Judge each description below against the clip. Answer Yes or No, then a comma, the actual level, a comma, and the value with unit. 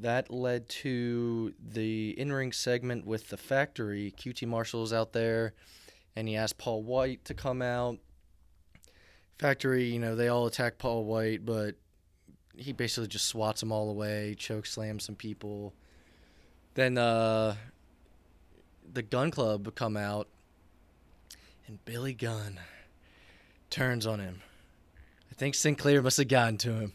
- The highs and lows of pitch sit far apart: No, average, 3.8 semitones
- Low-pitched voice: Yes, low, 110 Hz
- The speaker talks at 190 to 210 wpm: No, average, 140 wpm